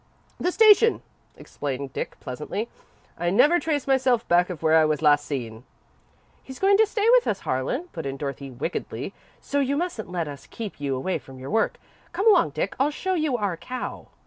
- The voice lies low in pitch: No, high, 195 Hz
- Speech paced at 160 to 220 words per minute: Yes, average, 200 wpm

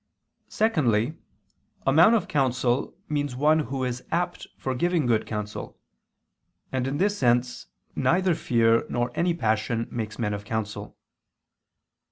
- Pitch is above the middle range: No, low, 125 Hz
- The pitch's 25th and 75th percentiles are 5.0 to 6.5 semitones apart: Yes, wide, 5.4 semitones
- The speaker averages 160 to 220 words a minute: No, slow, 135 wpm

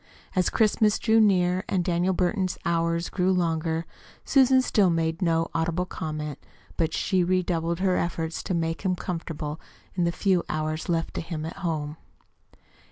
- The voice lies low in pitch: No, medium, 170 Hz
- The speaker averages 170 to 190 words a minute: No, average, 155 wpm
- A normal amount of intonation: No, narrow, 2.2 semitones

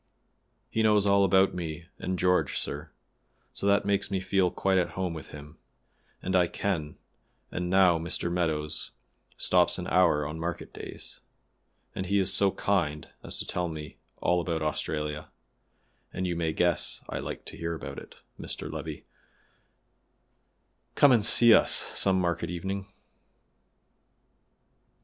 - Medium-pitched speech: No, very low, 90 Hz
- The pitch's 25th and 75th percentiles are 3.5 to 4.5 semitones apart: No, average, 3.0 semitones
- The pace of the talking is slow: No, average, 145 wpm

